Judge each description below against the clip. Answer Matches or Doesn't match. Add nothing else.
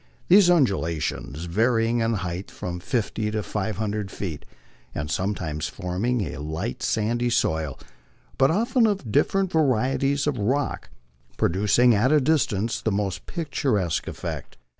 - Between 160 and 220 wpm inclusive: Doesn't match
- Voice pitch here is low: Matches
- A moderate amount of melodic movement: Doesn't match